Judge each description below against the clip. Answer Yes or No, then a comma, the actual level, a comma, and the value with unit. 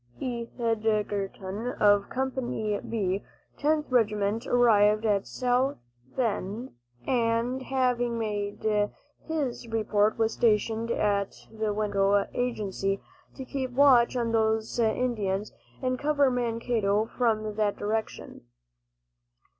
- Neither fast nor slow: No, slow, 100 wpm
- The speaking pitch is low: No, high, 225 Hz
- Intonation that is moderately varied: Yes, average, 3.0 semitones